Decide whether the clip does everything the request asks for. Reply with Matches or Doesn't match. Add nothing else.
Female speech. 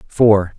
Doesn't match